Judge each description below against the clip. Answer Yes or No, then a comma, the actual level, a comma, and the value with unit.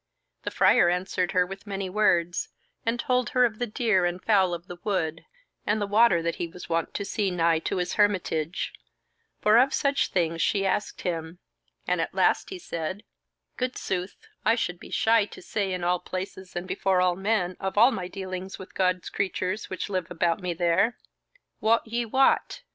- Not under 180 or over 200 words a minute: Yes, average, 195 wpm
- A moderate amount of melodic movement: Yes, average, 3.2 semitones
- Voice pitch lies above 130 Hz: Yes, high, 190 Hz